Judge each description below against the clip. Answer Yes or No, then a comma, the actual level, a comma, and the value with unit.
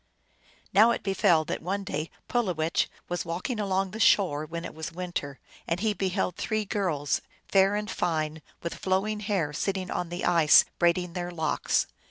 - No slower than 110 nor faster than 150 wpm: No, average, 170 wpm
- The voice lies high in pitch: No, medium, 180 Hz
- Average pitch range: Yes, average, 3.2 semitones